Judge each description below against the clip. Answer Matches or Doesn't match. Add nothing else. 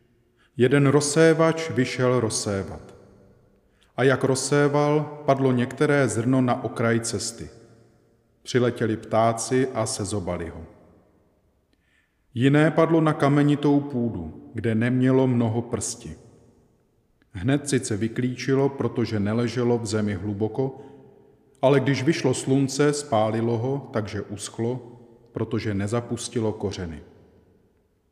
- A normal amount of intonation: Matches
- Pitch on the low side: Matches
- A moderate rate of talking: Doesn't match